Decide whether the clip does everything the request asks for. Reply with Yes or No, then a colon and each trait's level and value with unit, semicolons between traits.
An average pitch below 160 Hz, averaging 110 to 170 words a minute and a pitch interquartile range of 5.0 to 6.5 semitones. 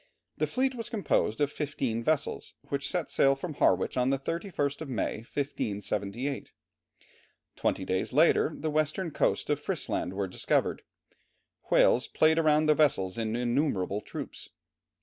Yes: medium, 140 Hz; average, 145 wpm; wide, 5.4 semitones